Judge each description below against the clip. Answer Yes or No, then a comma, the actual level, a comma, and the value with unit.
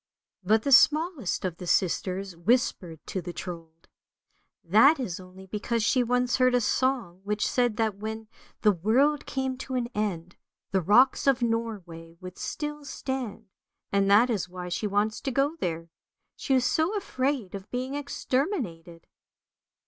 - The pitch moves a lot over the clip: Yes, wide, 5.9 semitones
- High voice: Yes, high, 220 Hz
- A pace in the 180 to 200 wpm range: No, average, 165 wpm